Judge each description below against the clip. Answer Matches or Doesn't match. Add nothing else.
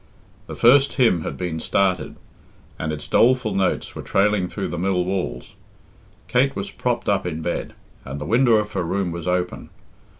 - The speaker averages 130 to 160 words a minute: Doesn't match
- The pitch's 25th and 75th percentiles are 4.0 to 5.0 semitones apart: Doesn't match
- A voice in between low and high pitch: Doesn't match